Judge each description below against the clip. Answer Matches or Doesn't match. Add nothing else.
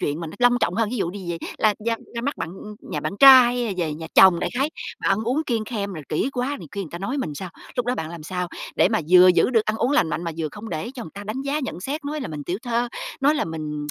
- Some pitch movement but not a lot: Doesn't match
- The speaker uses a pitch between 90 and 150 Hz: Doesn't match